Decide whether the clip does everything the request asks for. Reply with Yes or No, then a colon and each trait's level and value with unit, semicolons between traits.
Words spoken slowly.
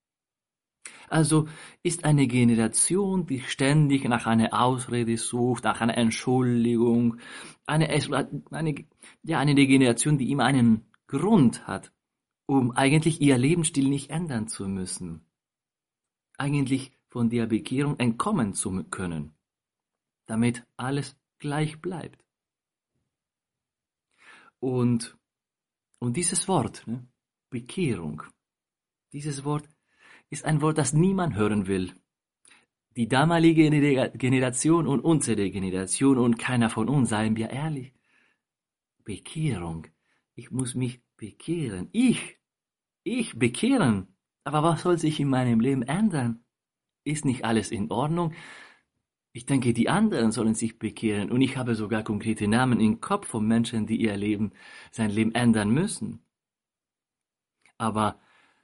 Yes: slow, 120 wpm